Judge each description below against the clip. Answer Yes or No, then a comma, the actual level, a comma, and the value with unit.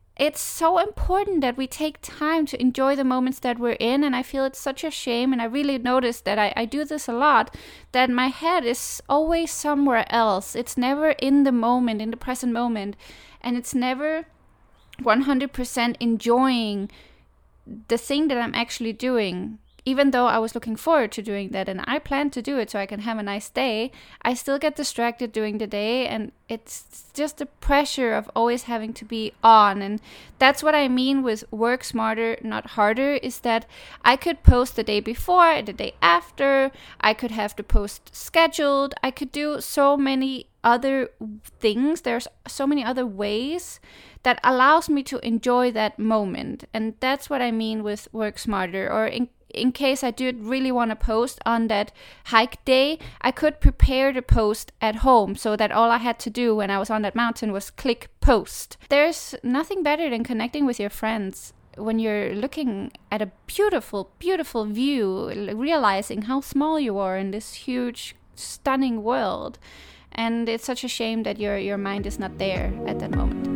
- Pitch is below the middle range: No, high, 245 Hz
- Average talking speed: Yes, average, 190 wpm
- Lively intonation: No, average, 3.7 semitones